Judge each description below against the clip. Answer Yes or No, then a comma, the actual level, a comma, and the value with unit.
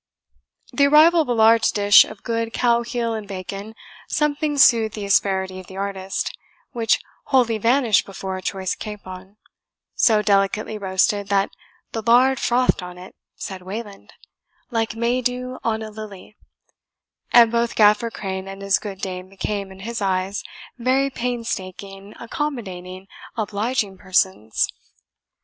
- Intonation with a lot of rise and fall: No, average, 3.4 semitones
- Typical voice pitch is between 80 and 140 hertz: No, high, 210 Hz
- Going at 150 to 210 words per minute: No, average, 140 wpm